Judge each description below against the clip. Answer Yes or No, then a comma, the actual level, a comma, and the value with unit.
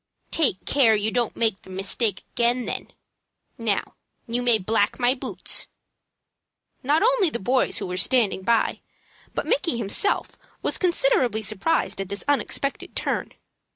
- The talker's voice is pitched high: Yes, high, 235 Hz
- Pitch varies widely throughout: No, average, 5.0 semitones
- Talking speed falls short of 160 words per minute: Yes, average, 145 wpm